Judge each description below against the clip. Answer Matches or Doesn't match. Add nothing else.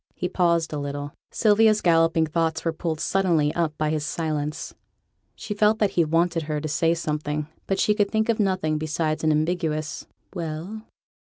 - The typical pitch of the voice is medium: Matches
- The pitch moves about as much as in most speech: Matches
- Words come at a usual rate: Matches